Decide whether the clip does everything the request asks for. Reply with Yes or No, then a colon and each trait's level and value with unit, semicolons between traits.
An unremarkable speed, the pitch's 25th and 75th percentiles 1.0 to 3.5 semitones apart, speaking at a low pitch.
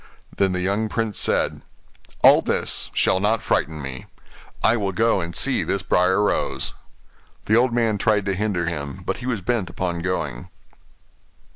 No: average, 165 wpm; average, 4.0 semitones; very low, 95 Hz